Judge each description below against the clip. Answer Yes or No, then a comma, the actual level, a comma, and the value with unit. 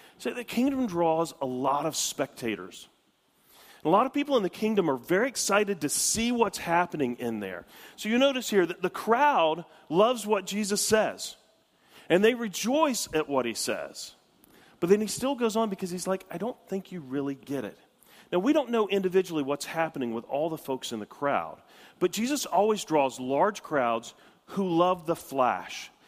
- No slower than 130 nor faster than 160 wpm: No, average, 190 wpm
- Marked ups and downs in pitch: Yes, wide, 7.4 semitones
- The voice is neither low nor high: Yes, medium, 180 Hz